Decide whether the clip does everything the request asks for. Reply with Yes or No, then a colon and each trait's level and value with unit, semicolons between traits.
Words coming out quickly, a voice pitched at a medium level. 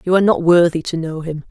Yes: fast, 280 wpm; medium, 170 Hz